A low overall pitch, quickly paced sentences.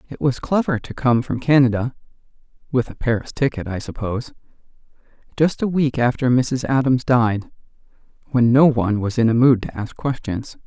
No: low, 125 Hz; average, 170 wpm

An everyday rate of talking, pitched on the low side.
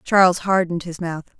No: average, 175 wpm; medium, 175 Hz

